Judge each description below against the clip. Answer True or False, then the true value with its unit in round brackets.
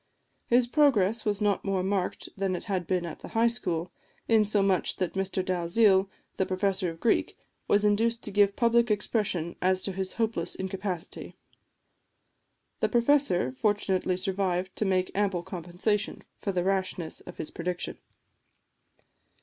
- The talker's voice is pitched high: True (195 Hz)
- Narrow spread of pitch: True (2.3 semitones)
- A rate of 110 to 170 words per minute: True (145 wpm)